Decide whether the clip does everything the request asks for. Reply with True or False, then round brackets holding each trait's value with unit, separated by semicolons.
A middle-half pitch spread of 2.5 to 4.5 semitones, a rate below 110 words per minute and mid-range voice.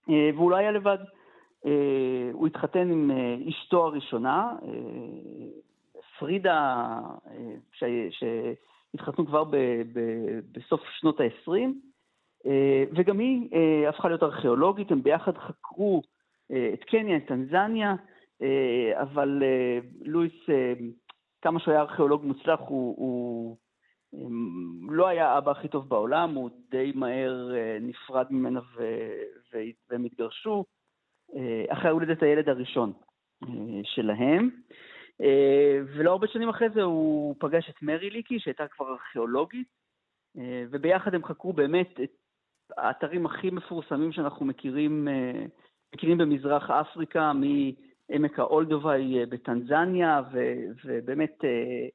False (5.2 semitones; 100 wpm; 150 Hz)